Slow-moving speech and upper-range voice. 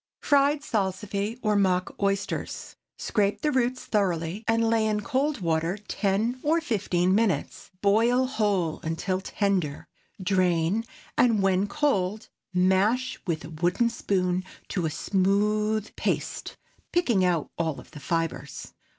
Yes: slow, 130 wpm; high, 200 Hz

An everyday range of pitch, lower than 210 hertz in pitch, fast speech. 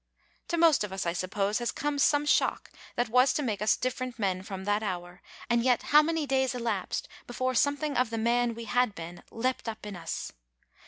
No: average, 4.3 semitones; high, 235 Hz; fast, 210 wpm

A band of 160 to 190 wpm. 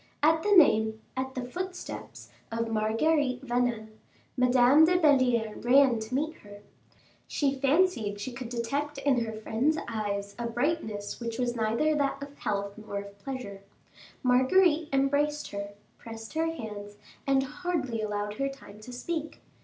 No: average, 150 wpm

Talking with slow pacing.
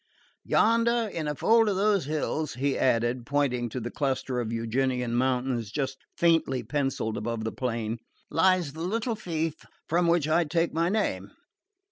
No: average, 160 wpm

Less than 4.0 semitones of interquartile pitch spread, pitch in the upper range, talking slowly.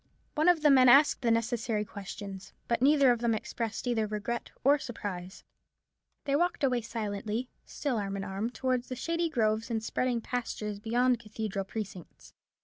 No: average, 3.3 semitones; high, 230 Hz; average, 170 wpm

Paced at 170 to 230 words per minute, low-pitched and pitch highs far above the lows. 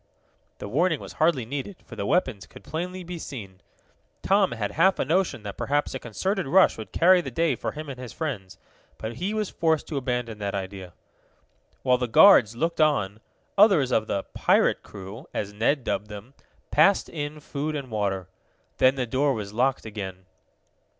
Yes: average, 185 wpm; low, 130 Hz; wide, 7.4 semitones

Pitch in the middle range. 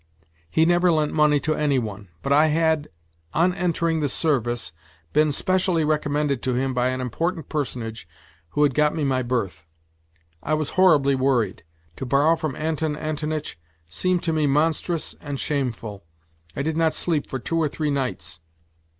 Yes: medium, 150 Hz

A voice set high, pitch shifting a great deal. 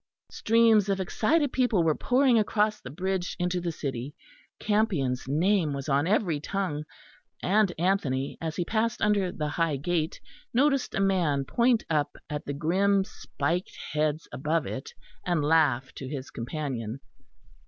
No: medium, 170 Hz; wide, 5.8 semitones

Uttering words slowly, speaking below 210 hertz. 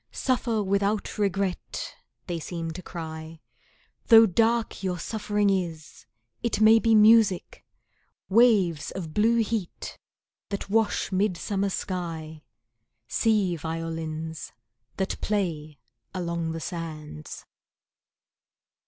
Yes: slow, 100 wpm; high, 190 Hz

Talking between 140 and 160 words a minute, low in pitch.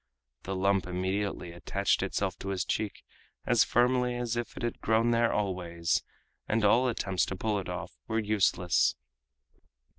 Yes: average, 155 wpm; low, 100 Hz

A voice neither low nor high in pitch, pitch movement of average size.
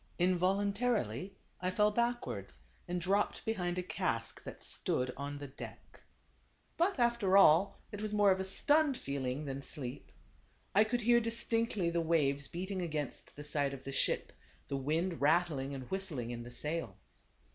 No: medium, 175 Hz; wide, 6.6 semitones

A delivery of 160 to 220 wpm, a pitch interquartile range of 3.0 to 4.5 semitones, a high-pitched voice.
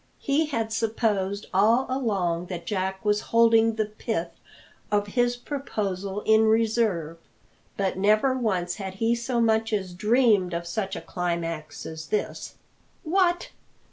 No: average, 140 wpm; average, 3.6 semitones; high, 210 Hz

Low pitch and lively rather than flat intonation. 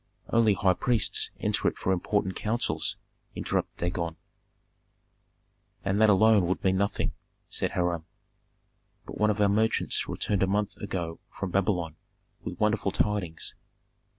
No: low, 100 Hz; average, 2.8 semitones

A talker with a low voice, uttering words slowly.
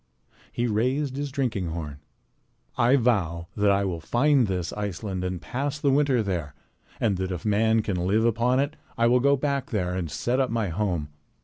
No: low, 110 Hz; average, 190 wpm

